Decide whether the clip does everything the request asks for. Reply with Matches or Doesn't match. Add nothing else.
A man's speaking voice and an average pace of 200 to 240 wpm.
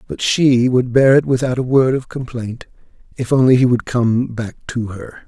Matches